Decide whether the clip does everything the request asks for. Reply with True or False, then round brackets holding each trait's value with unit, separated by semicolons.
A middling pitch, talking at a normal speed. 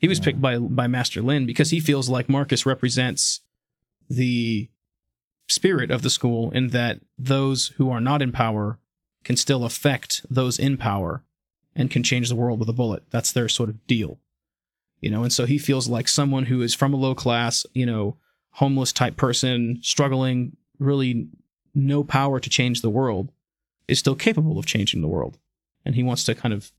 False (125 Hz; 190 wpm)